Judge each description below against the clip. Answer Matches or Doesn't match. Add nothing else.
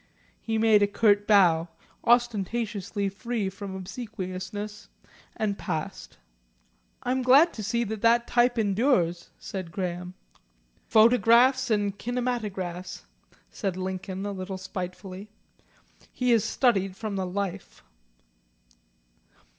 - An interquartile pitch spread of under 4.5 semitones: Matches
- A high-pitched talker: Matches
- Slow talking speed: Matches